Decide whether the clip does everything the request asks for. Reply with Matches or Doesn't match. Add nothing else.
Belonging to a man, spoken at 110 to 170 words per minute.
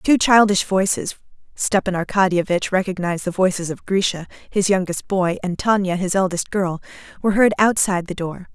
Doesn't match